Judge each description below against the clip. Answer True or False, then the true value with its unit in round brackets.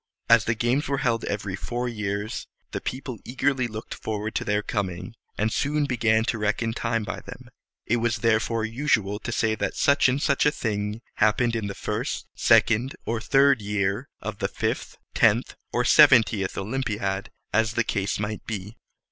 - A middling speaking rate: True (180 wpm)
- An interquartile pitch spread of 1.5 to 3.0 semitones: True (2.7 semitones)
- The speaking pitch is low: True (110 Hz)